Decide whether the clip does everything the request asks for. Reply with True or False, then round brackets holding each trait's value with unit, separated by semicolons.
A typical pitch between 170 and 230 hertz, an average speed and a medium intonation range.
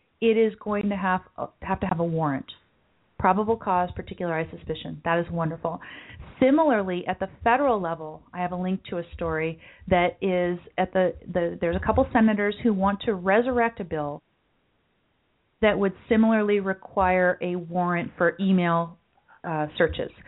True (185 Hz; 160 wpm; 3.3 semitones)